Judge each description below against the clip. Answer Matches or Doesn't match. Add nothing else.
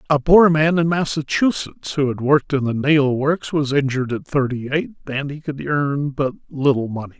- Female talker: Doesn't match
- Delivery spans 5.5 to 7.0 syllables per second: Doesn't match